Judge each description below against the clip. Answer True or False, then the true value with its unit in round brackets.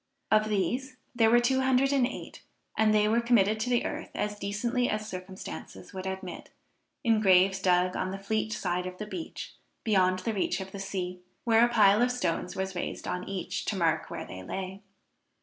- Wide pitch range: False (3.7 semitones)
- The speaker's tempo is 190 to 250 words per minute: True (200 wpm)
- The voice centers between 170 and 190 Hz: False (200 Hz)